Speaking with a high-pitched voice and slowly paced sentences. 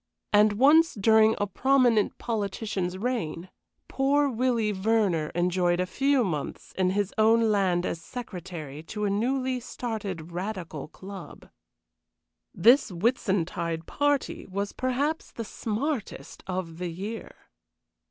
Yes: high, 205 Hz; slow, 120 wpm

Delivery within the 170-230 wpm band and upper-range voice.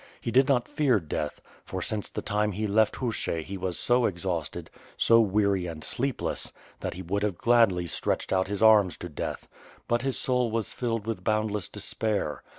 No: average, 190 wpm; low, 105 Hz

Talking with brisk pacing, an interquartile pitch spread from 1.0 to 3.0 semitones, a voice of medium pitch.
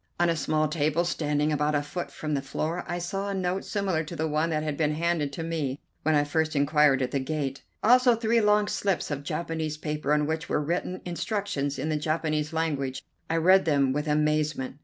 Yes: fast, 215 wpm; narrow, 2.6 semitones; medium, 155 Hz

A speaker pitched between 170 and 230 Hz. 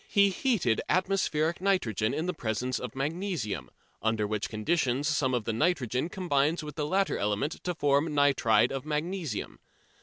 No: medium, 145 Hz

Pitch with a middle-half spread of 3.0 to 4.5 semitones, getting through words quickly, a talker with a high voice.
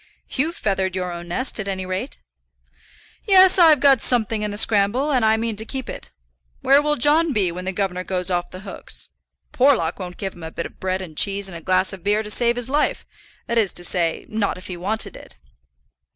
No: average, 5.1 semitones; fast, 225 wpm; high, 205 Hz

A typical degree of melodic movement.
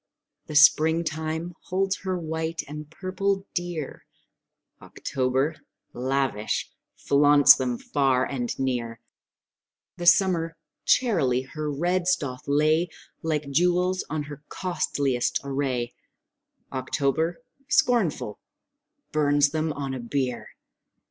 Yes: average, 4.2 semitones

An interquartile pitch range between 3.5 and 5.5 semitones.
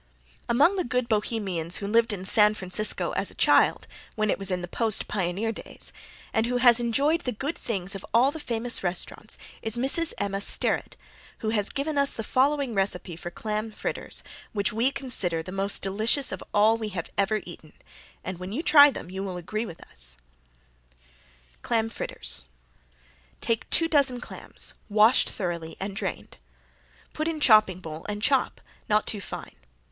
Yes: average, 4.2 semitones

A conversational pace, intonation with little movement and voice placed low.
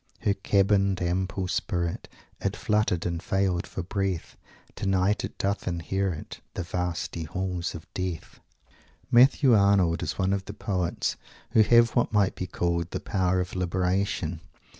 Yes: average, 145 wpm; narrow, 2.1 semitones; very low, 95 Hz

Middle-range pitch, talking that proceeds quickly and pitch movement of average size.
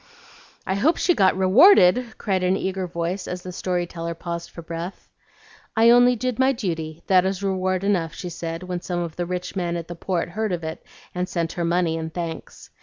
No: medium, 180 Hz; fast, 210 wpm; narrow, 2.2 semitones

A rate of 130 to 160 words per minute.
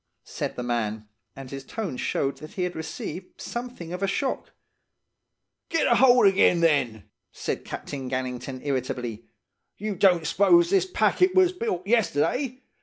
Yes: average, 150 wpm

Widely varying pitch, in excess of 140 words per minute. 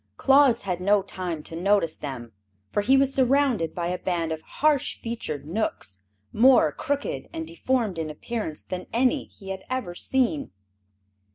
Yes: wide, 7.8 semitones; average, 160 wpm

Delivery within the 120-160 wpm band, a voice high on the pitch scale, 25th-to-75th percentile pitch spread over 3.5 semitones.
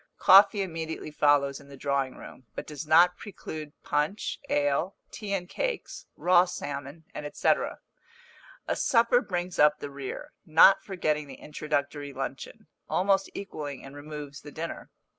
No: average, 140 wpm; medium, 150 Hz; average, 4.1 semitones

